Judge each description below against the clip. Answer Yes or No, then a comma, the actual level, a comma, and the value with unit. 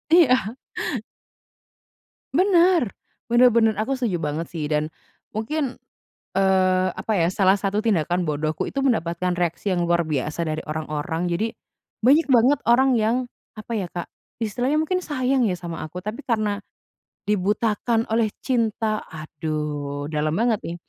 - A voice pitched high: Yes, high, 205 Hz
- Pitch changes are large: Yes, wide, 6.1 semitones